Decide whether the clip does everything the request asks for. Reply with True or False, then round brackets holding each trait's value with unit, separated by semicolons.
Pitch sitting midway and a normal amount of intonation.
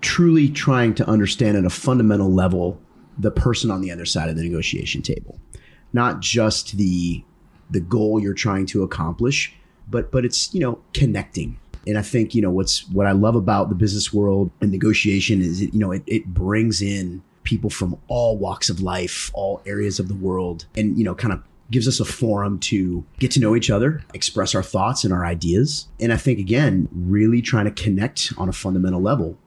False (100 Hz; 3.5 semitones)